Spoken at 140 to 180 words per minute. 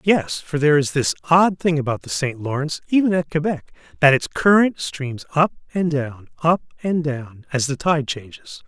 No: average, 195 wpm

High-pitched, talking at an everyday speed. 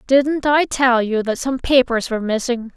Yes: very high, 250 Hz; average, 195 wpm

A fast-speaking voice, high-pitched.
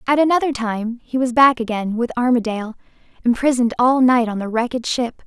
No: average, 180 wpm; high, 240 Hz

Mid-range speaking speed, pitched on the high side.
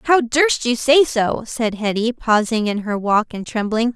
Yes: average, 195 wpm; high, 235 Hz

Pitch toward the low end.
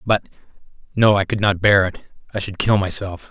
Yes: low, 100 Hz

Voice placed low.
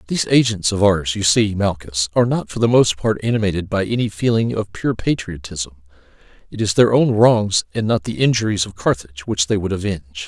Yes: low, 100 Hz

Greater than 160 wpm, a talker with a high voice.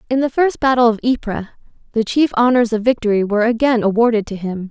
Yes: fast, 205 wpm; high, 230 Hz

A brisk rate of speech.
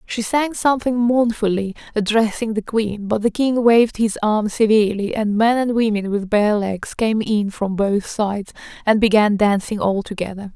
No: average, 175 wpm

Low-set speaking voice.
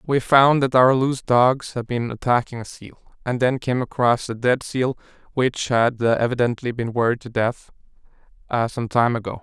Yes: low, 125 Hz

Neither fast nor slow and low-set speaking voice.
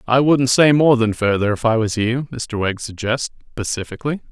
Yes: average, 195 wpm; low, 120 Hz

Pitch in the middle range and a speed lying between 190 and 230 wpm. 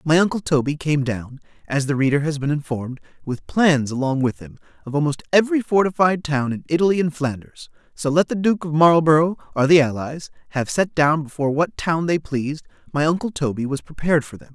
Yes: medium, 150 Hz; average, 200 wpm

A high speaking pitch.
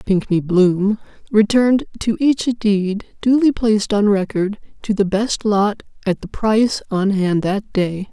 Yes: high, 205 Hz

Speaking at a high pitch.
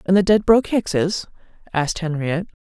No: medium, 180 Hz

